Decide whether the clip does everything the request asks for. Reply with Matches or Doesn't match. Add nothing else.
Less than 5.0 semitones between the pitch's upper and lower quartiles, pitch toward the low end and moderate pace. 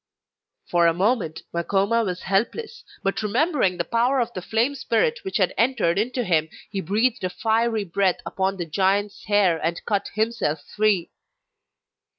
Doesn't match